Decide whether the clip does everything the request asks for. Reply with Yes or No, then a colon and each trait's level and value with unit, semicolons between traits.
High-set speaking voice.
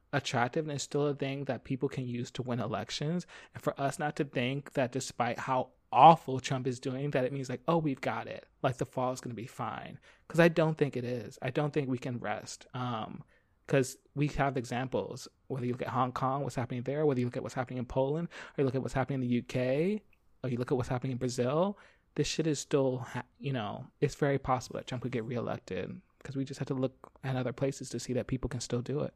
No: low, 130 Hz